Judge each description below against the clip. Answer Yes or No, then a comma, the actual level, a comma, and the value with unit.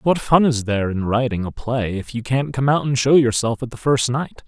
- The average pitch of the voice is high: No, low, 125 Hz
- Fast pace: Yes, fast, 270 wpm